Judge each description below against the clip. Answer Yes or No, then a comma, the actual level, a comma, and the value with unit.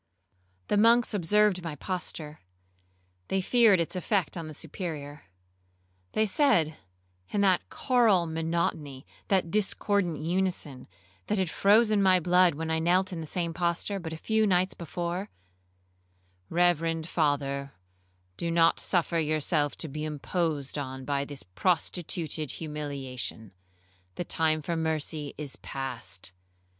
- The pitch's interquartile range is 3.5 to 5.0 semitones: Yes, average, 4.2 semitones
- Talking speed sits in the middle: No, slow, 125 wpm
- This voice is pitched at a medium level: Yes, medium, 165 Hz